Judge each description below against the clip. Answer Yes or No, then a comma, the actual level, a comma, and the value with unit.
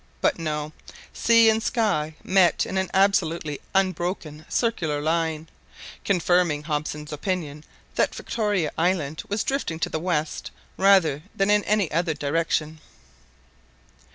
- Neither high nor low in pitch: Yes, medium, 165 Hz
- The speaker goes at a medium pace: No, slow, 125 wpm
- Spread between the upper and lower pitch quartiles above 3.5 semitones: Yes, average, 4.1 semitones